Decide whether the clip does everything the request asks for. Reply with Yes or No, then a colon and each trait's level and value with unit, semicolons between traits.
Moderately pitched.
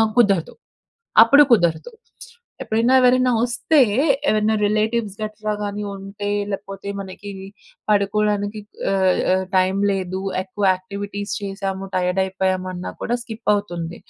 No: high, 200 Hz